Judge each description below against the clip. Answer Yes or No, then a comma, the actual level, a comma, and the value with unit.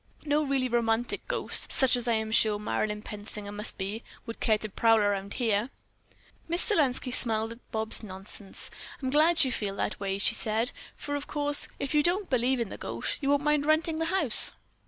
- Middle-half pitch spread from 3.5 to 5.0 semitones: No, wide, 5.4 semitones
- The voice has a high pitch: Yes, high, 235 Hz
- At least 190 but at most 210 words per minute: Yes, average, 200 wpm